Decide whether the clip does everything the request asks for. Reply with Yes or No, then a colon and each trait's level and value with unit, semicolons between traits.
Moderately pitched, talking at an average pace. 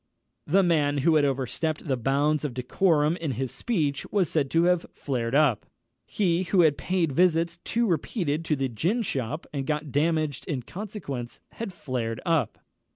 Yes: medium, 155 Hz; average, 170 wpm